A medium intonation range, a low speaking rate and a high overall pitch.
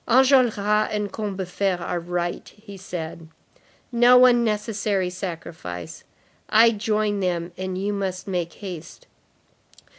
Yes: average, 3.3 semitones; slow, 110 wpm; high, 195 Hz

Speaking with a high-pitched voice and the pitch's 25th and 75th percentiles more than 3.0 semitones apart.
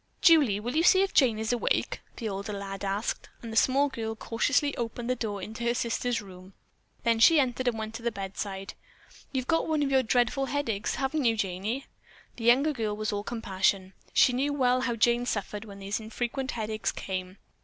Yes: high, 230 Hz; average, 3.9 semitones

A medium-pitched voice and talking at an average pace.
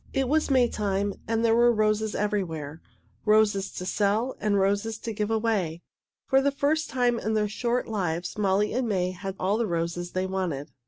No: high, 210 Hz; average, 180 wpm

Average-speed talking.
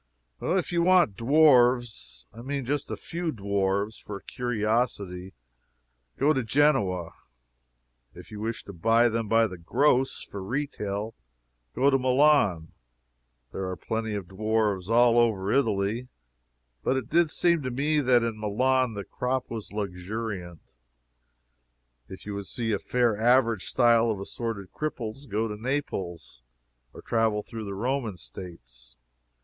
Yes: average, 145 wpm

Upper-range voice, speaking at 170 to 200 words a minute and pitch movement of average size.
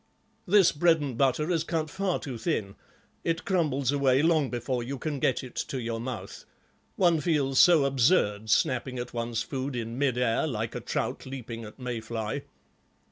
No: low, 130 Hz; average, 180 wpm; average, 4.6 semitones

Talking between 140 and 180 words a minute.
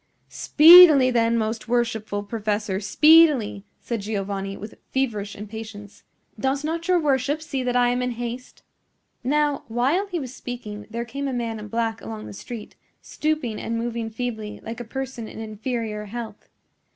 Yes: average, 160 wpm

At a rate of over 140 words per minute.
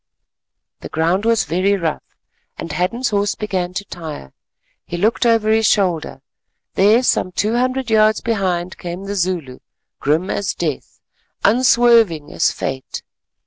No: slow, 135 wpm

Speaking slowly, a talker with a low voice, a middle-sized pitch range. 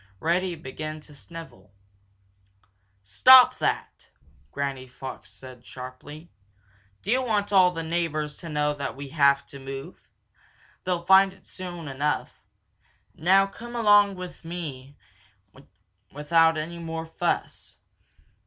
No: slow, 120 wpm; medium, 165 Hz; average, 4.7 semitones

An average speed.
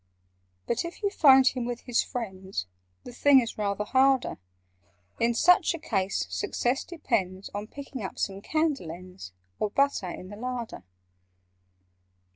Yes: average, 145 wpm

